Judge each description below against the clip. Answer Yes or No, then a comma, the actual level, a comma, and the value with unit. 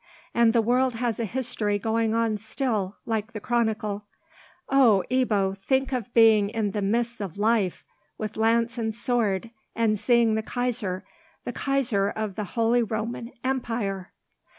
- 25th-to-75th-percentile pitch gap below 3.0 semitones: Yes, narrow, 2.5 semitones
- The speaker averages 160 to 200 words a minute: No, average, 150 wpm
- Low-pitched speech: No, high, 225 Hz